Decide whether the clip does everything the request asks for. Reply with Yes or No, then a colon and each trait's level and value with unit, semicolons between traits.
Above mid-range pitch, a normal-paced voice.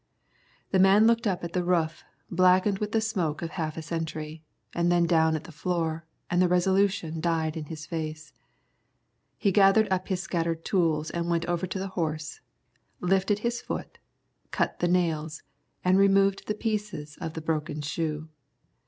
No: medium, 170 Hz; average, 170 wpm